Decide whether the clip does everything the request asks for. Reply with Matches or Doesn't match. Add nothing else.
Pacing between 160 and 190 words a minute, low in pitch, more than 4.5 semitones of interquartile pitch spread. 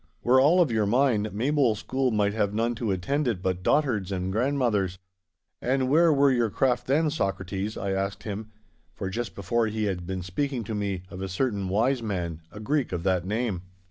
Doesn't match